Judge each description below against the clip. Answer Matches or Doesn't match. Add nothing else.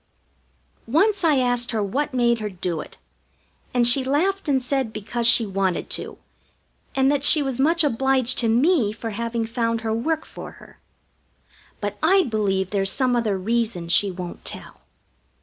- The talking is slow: Doesn't match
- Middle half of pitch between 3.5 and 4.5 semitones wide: Matches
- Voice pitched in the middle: Doesn't match